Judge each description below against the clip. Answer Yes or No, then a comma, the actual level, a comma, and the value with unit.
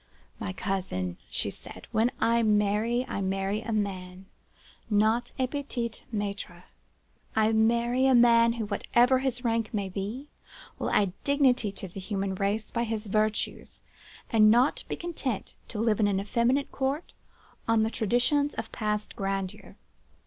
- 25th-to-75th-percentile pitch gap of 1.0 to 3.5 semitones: Yes, average, 3.2 semitones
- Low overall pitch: No, high, 220 Hz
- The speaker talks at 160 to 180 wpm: No, average, 150 wpm